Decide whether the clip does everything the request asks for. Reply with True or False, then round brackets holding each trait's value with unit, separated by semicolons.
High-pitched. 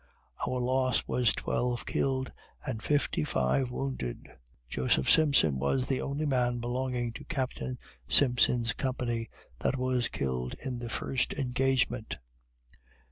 False (125 Hz)